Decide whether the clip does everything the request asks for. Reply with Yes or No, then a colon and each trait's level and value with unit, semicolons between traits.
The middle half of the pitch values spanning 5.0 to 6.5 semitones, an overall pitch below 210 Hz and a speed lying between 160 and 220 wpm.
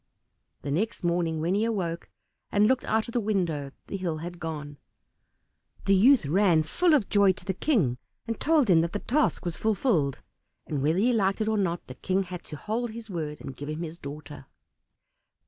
Yes: wide, 5.5 semitones; medium, 185 Hz; fast, 205 wpm